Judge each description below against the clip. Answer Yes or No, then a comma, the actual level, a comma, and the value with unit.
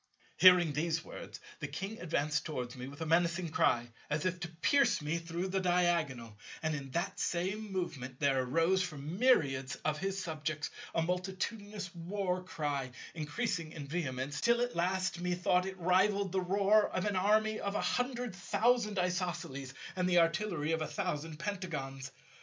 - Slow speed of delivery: No, average, 165 wpm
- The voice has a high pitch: No, medium, 175 Hz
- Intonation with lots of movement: No, average, 4.1 semitones